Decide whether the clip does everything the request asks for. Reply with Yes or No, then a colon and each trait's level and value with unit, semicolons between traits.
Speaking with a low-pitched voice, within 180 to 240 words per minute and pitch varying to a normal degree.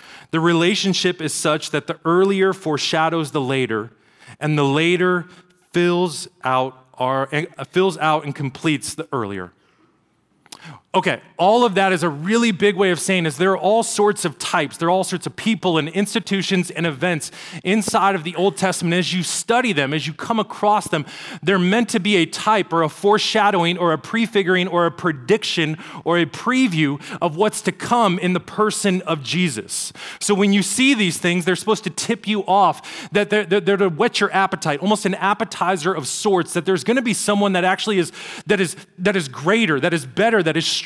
No: medium, 180 Hz; average, 200 wpm; average, 4.1 semitones